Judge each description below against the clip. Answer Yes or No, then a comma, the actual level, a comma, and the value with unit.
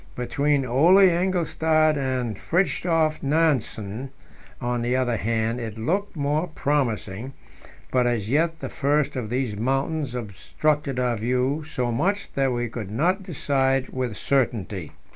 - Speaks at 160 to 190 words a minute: No, slow, 135 wpm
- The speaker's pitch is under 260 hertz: Yes, low, 135 Hz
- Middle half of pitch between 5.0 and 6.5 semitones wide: No, average, 4.5 semitones